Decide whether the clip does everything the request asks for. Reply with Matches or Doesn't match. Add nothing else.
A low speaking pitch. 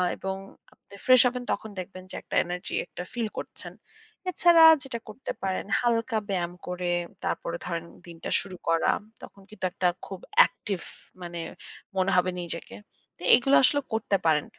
Doesn't match